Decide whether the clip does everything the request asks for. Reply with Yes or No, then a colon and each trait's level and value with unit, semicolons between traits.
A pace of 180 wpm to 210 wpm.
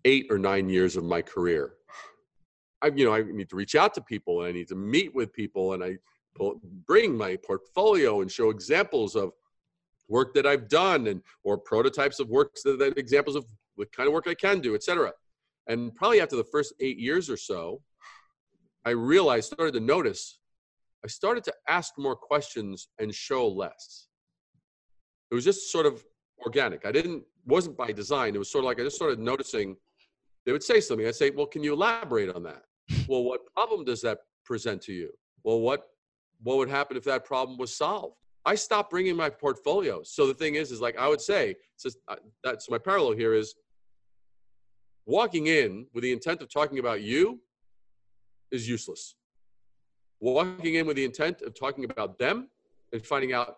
Yes: average, 190 wpm